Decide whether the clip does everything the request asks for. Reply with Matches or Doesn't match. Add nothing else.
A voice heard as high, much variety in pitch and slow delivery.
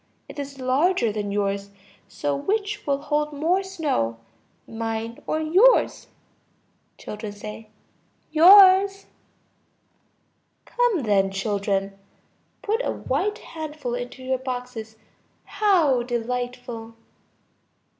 Matches